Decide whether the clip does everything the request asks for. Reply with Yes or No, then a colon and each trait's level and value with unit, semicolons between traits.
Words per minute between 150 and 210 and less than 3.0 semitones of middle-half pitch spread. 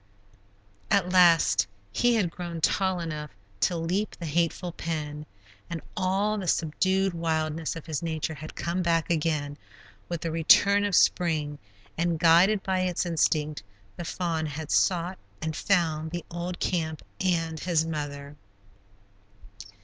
No: average, 140 wpm; narrow, 2.5 semitones